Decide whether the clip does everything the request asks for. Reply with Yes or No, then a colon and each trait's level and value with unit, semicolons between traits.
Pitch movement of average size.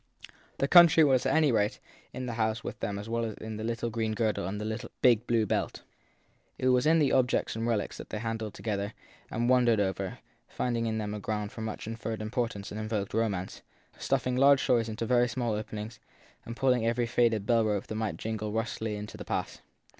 No: narrow, 2.2 semitones